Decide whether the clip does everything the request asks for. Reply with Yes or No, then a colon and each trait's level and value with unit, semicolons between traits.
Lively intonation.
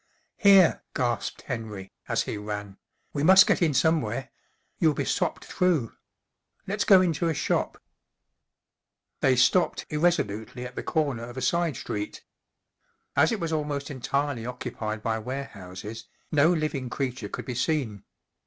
Yes: wide, 5.9 semitones